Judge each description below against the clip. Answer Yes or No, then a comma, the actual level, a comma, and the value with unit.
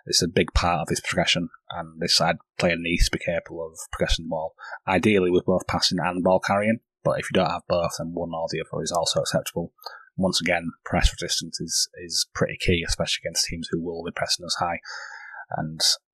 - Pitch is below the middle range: Yes, very low, 90 Hz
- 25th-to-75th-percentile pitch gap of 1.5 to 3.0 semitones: No, average, 5.2 semitones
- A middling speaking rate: No, fast, 215 wpm